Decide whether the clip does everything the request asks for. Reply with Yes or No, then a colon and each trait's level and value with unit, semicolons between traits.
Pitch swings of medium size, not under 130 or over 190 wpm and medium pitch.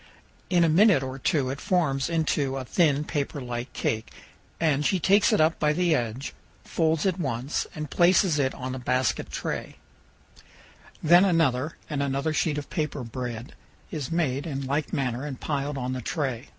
Yes: average, 3.7 semitones; average, 175 wpm; medium, 145 Hz